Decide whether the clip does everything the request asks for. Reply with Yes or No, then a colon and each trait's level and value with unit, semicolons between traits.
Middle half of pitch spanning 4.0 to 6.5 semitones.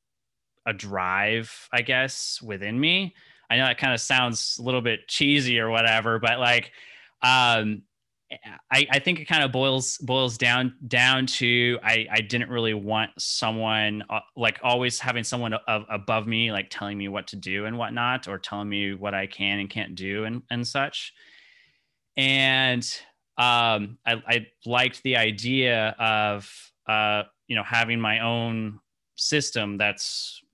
No: average, 3.1 semitones